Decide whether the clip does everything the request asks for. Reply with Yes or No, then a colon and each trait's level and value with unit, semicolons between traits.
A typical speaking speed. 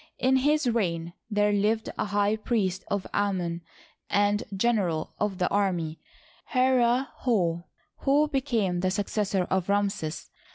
No: slow, 125 wpm